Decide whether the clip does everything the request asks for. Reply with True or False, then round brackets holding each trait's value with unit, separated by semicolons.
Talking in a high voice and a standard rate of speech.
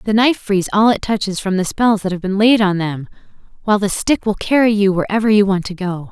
False (200 Hz; 255 wpm)